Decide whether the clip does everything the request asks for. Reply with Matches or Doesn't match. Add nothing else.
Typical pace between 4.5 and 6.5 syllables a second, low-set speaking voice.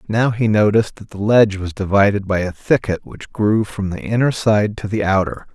Matches